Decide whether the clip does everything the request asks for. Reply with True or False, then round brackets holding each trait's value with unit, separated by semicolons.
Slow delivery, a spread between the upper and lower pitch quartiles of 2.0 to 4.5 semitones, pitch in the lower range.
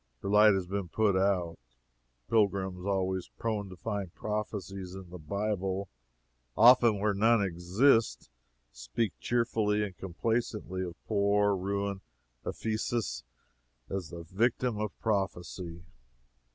True (120 wpm; 2.5 semitones; 100 Hz)